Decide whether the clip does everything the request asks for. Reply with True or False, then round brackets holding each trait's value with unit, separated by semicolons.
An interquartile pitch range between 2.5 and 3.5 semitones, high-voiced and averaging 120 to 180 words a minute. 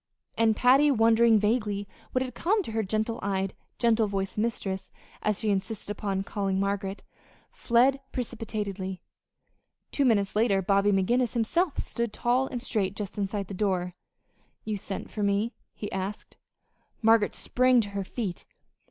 True (3.0 semitones; 210 Hz; 150 wpm)